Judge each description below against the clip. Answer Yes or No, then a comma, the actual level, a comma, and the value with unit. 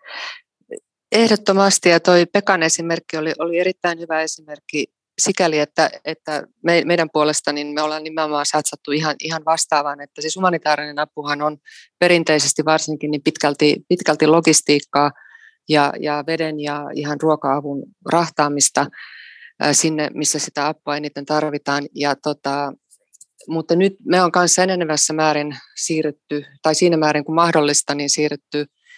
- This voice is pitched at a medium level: Yes, medium, 155 Hz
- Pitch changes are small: Yes, narrow, 2.2 semitones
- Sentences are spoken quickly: No, average, 130 wpm